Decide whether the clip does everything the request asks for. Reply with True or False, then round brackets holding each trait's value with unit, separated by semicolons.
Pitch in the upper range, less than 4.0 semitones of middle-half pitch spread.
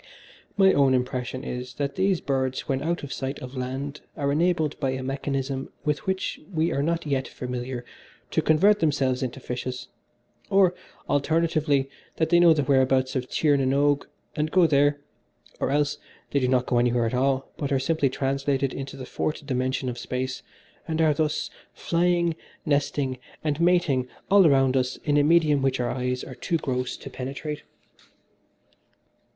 False (140 Hz; 3.1 semitones)